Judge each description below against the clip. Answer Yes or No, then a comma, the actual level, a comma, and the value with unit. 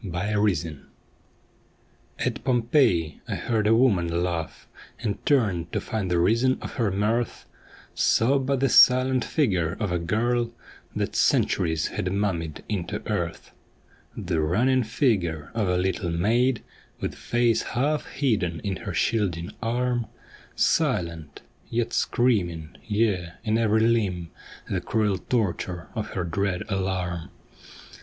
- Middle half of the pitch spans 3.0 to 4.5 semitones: No, average, 5.2 semitones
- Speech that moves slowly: Yes, slow, 130 wpm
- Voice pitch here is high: No, low, 105 Hz